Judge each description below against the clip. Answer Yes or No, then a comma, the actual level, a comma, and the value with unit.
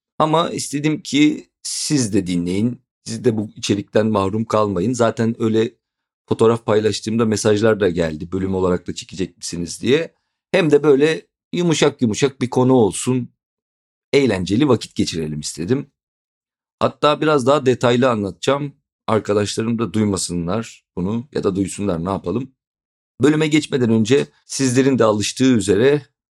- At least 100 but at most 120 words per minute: No, average, 130 wpm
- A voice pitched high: No, low, 115 Hz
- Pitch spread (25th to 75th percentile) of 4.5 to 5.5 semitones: Yes, average, 5.0 semitones